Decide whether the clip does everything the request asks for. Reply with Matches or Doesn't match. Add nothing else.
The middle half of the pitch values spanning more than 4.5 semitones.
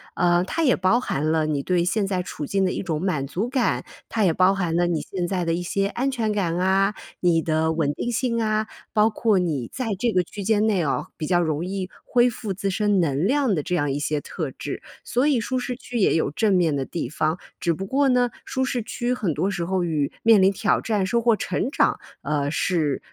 Matches